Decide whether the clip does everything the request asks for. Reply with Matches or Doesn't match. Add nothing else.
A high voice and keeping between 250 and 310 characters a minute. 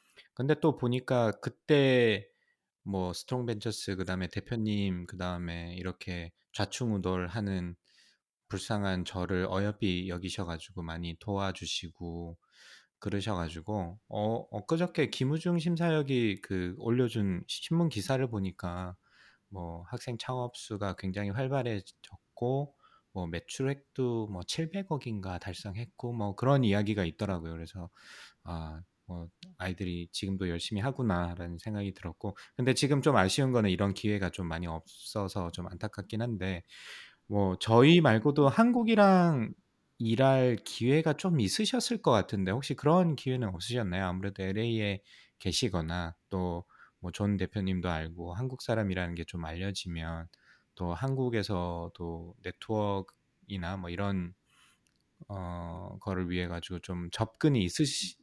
Doesn't match